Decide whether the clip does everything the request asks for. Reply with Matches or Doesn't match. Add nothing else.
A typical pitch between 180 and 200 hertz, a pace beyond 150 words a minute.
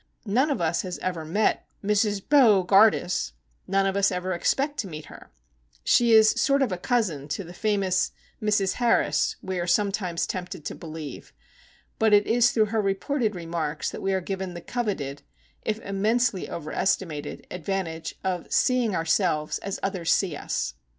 Matches